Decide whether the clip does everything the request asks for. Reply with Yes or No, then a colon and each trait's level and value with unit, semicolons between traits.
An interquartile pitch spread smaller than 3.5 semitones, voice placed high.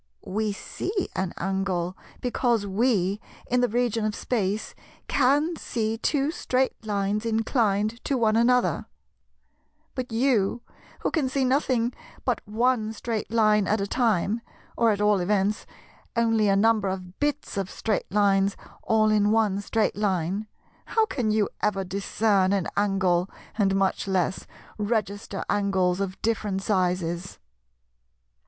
Yes: average, 3.1 semitones; high, 210 Hz